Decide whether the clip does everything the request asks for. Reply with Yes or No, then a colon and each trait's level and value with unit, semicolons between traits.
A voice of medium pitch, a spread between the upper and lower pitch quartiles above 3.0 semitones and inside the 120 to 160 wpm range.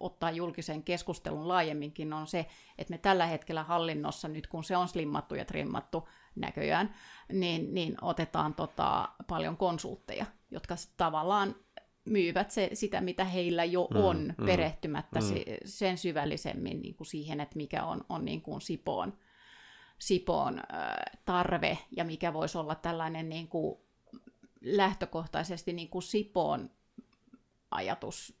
No: medium, 175 Hz; narrow, 2.5 semitones; average, 130 wpm